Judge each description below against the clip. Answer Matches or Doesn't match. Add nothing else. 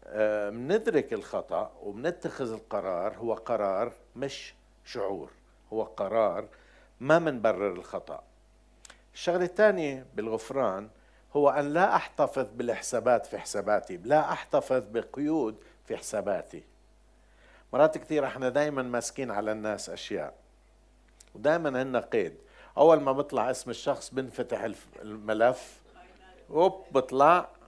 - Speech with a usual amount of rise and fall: Doesn't match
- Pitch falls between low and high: Doesn't match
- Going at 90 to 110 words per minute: Matches